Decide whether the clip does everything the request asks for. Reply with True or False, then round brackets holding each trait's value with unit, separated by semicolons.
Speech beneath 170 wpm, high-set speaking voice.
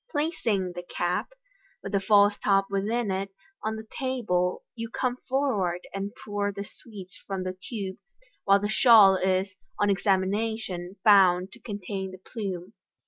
True (150 wpm; 200 Hz)